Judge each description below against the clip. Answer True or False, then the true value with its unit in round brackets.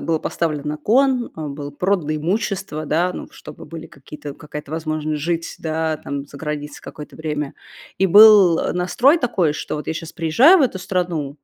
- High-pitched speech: False (160 Hz)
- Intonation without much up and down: False (3.8 semitones)